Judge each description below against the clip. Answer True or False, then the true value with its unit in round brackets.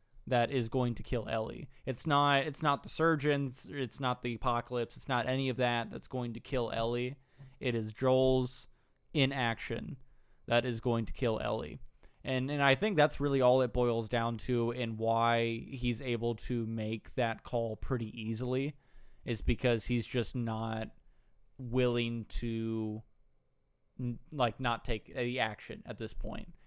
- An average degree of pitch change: False (2.2 semitones)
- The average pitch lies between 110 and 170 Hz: True (120 Hz)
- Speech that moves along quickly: False (160 wpm)